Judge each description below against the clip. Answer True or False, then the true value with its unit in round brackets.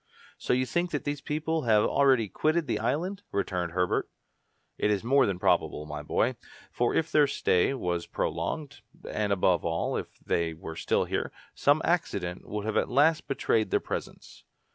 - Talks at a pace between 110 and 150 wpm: False (175 wpm)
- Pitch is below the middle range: True (120 Hz)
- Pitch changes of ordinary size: False (8.3 semitones)